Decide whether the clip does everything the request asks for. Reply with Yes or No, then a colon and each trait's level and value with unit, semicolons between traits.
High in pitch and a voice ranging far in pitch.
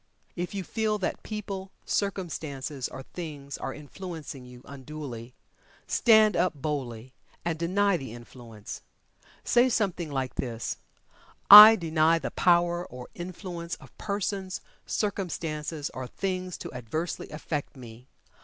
No: medium, 165 Hz; wide, 5.9 semitones